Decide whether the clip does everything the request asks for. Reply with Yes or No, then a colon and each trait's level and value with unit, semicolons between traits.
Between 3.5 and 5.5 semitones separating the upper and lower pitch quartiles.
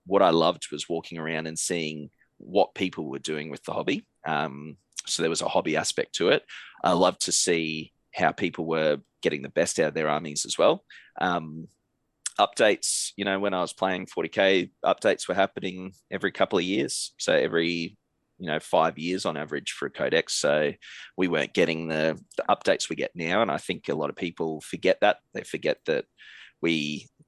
No: narrow, 2.5 semitones